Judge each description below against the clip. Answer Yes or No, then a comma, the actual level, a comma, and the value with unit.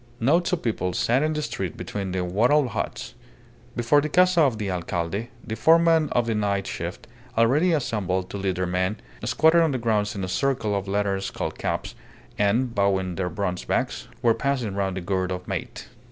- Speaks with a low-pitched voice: Yes, low, 105 Hz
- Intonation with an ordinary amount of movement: No, wide, 6.2 semitones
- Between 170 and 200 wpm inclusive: Yes, average, 195 wpm